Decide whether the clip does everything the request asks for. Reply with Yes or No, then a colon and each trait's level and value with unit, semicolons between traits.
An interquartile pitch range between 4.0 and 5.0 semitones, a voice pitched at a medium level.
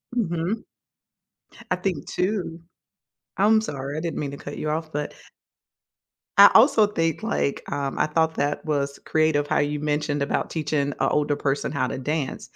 No: average, 3.1 semitones; medium, 155 Hz